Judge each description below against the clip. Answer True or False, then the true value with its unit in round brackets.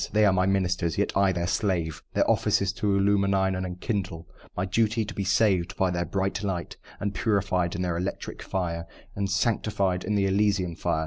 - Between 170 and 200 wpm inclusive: True (195 wpm)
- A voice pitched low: True (95 Hz)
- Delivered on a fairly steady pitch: True (2.1 semitones)